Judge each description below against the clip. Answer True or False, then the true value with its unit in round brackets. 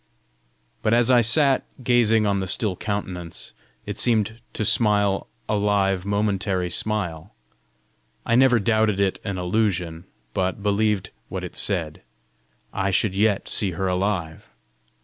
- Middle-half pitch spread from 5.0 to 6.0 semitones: False (2.7 semitones)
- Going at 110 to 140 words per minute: True (135 wpm)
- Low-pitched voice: True (100 Hz)